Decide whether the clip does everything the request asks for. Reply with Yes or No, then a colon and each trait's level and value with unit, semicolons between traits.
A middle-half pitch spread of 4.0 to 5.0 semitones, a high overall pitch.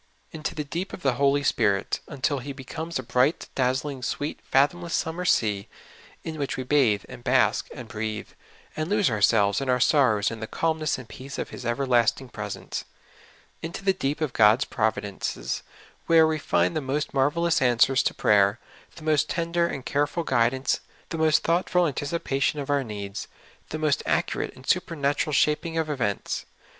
No: average, 4.7 semitones; medium, 140 Hz